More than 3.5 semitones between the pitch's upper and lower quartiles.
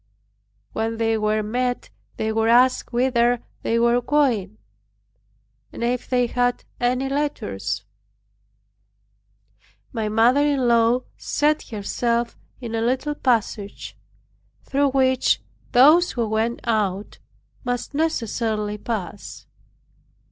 No: average, 2.7 semitones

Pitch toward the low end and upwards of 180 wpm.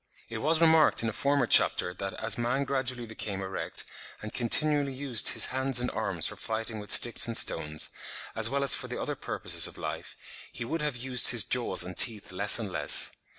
Yes: low, 120 Hz; fast, 205 wpm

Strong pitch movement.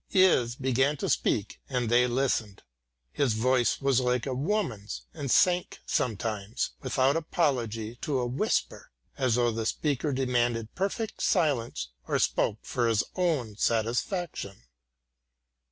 No: average, 3.6 semitones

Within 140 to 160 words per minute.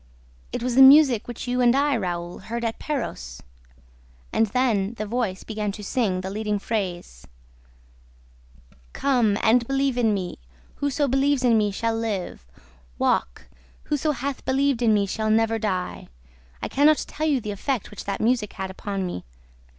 No: average, 170 wpm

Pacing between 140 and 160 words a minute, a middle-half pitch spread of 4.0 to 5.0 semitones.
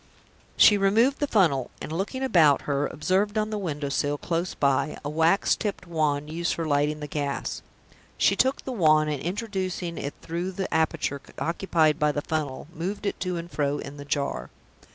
No: average, 185 wpm; average, 4.6 semitones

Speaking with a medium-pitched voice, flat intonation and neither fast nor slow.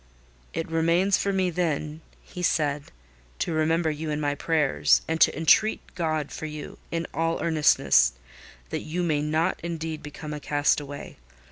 Yes: medium, 160 Hz; narrow, 1.9 semitones; average, 155 wpm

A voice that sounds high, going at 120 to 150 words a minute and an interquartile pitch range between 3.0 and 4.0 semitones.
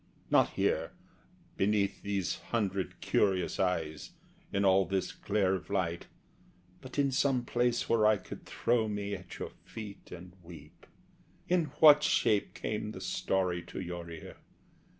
No: low, 100 Hz; average, 145 wpm; average, 3.5 semitones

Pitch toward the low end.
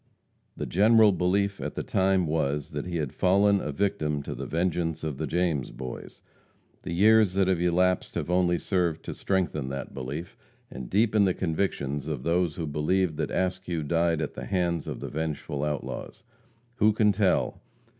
Yes: very low, 85 Hz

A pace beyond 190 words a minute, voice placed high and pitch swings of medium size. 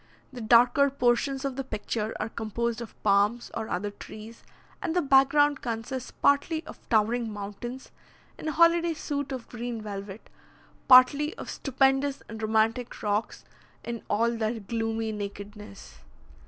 No: average, 145 wpm; high, 235 Hz; average, 3.8 semitones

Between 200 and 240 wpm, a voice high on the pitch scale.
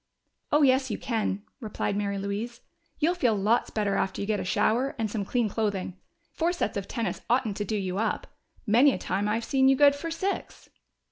Yes: fast, 205 wpm; high, 220 Hz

